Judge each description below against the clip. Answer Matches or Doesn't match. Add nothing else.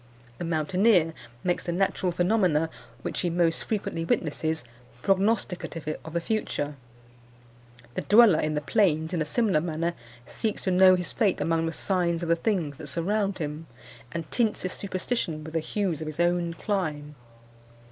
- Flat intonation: Doesn't match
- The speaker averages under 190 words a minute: Matches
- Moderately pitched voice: Matches